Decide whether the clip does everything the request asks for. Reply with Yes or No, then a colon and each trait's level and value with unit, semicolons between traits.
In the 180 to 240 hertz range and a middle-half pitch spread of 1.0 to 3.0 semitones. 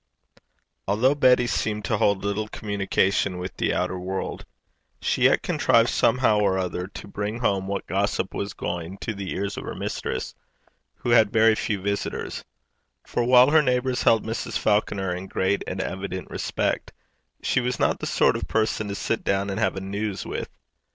No: low, 100 Hz; average, 2.7 semitones